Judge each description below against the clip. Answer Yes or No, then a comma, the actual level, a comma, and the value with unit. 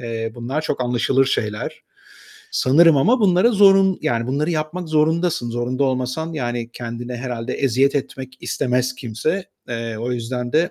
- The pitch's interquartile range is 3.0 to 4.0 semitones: No, average, 4.7 semitones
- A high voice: No, low, 130 Hz